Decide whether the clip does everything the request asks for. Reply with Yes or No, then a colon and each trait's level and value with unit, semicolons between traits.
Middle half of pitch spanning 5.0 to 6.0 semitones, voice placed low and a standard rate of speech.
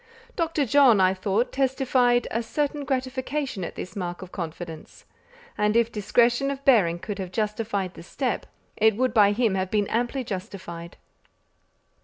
No: average, 5.3 semitones; high, 220 Hz; average, 155 wpm